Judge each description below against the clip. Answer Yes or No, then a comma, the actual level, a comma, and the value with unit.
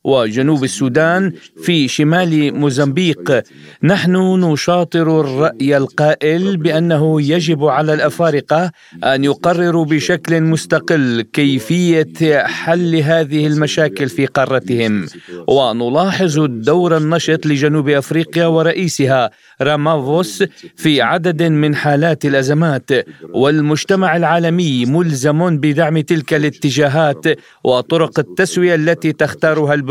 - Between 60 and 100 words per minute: Yes, average, 90 wpm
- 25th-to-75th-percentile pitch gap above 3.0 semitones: No, narrow, 2.4 semitones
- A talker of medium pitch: Yes, medium, 155 Hz